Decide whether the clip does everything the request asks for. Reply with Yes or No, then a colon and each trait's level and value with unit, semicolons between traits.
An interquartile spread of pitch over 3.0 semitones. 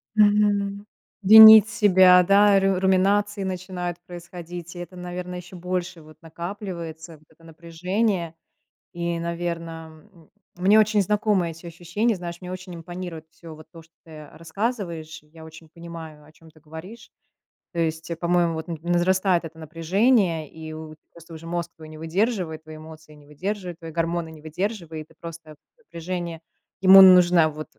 No: average, 2.7 semitones